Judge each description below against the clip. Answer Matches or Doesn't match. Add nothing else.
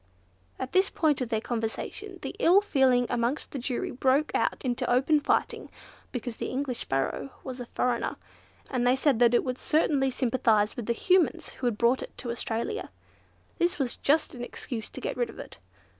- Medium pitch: Doesn't match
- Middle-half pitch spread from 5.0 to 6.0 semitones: Doesn't match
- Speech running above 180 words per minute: Matches